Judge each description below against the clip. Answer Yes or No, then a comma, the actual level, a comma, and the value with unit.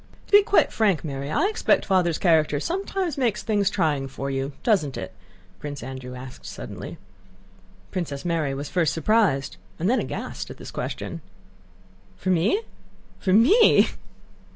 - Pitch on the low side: No, medium, 170 Hz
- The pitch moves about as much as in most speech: No, wide, 7.8 semitones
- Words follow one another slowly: No, average, 150 wpm